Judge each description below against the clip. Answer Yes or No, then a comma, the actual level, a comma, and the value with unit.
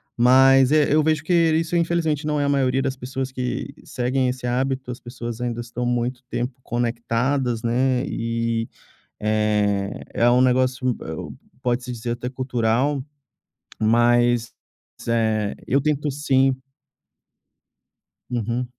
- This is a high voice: No, low, 125 Hz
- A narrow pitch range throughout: Yes, narrow, 2.2 semitones